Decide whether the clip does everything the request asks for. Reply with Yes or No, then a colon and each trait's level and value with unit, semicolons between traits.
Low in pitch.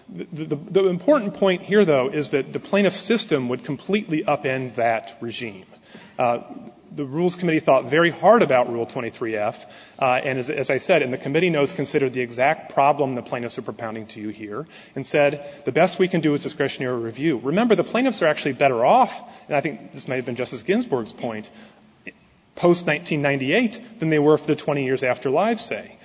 No: medium, 145 Hz